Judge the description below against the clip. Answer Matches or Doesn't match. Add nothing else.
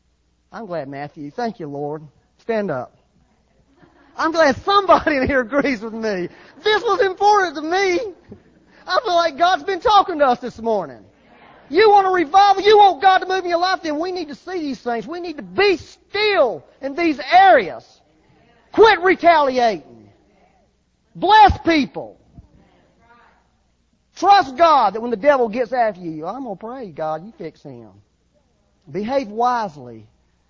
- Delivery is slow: Doesn't match